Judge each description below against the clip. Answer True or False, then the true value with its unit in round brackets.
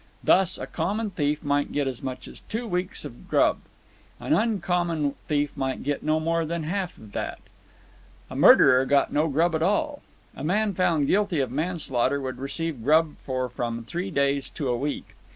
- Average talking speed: True (180 wpm)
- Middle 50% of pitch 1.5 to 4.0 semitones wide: False (4.4 semitones)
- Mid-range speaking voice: True (155 Hz)